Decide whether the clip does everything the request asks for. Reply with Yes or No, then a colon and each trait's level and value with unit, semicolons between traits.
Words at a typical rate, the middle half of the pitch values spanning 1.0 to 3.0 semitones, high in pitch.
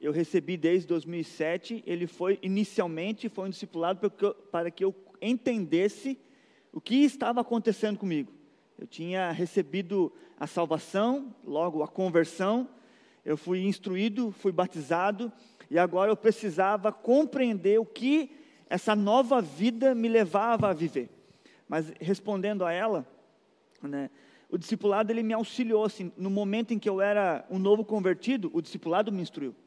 No: average, 150 wpm; average, 4.3 semitones; high, 200 Hz